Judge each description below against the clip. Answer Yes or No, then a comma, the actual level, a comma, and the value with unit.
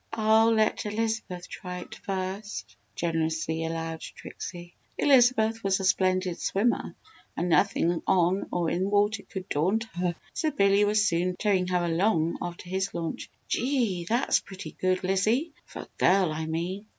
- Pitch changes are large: No, average, 3.6 semitones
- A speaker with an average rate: Yes, average, 150 wpm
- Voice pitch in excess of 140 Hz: Yes, high, 190 Hz